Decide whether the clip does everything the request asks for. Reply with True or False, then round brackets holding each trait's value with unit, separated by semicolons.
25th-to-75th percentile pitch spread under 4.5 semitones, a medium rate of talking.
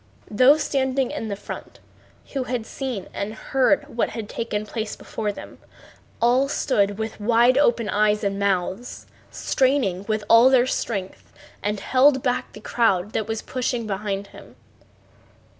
True (3.7 semitones; 145 wpm)